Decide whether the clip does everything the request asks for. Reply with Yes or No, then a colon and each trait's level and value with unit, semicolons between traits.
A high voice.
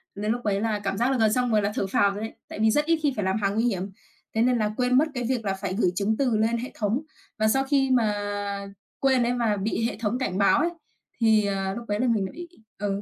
Yes: high, 220 Hz